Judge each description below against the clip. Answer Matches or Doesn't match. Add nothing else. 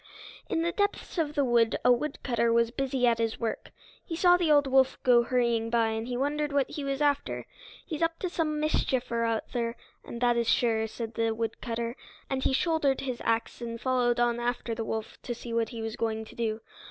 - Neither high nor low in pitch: Doesn't match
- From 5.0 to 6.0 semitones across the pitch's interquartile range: Doesn't match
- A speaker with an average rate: Doesn't match